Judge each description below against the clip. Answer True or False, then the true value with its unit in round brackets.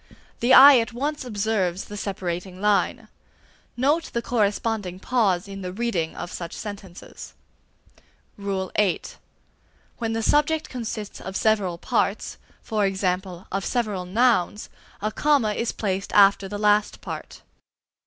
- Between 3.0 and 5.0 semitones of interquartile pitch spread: True (3.5 semitones)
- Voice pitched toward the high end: True (210 Hz)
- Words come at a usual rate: False (125 wpm)